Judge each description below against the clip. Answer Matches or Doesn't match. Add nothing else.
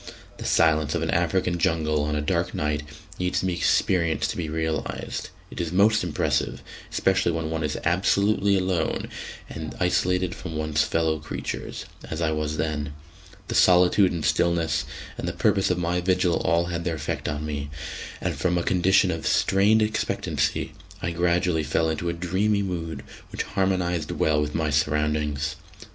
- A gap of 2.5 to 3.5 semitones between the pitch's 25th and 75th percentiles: Matches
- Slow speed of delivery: Doesn't match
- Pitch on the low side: Matches